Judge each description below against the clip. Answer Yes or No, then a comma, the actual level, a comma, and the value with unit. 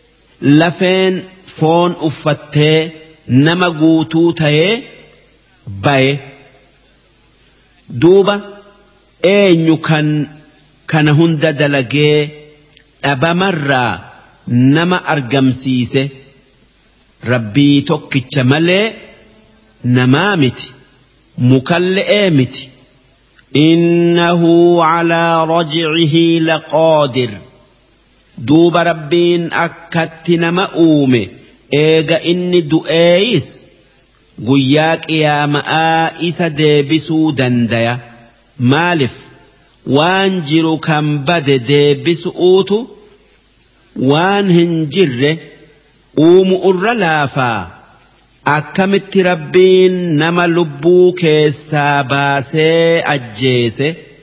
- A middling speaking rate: No, slow, 60 wpm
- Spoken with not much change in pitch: No, average, 3.5 semitones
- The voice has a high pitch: No, medium, 155 Hz